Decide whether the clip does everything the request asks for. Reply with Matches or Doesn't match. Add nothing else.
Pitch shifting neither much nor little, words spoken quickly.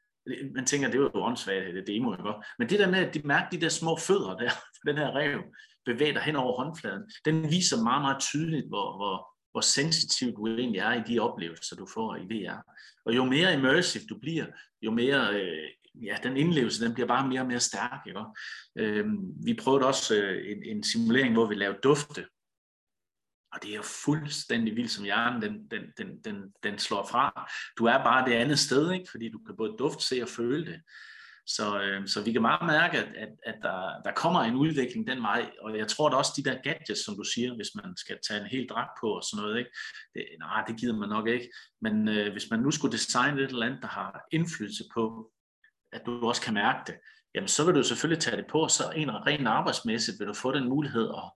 Doesn't match